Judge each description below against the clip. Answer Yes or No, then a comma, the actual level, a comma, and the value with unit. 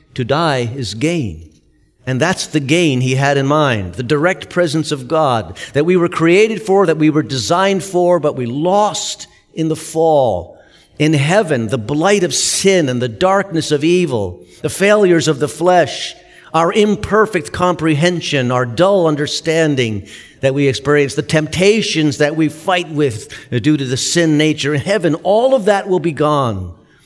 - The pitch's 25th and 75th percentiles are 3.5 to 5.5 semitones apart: Yes, average, 4.4 semitones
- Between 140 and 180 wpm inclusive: Yes, average, 170 wpm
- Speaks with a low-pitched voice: No, medium, 155 Hz